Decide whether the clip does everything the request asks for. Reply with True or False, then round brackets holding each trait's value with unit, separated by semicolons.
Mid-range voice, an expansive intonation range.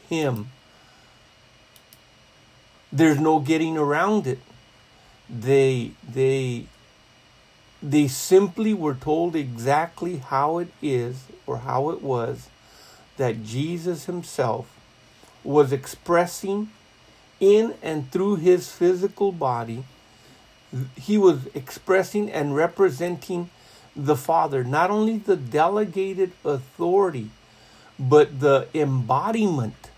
True (145 Hz; 5.7 semitones)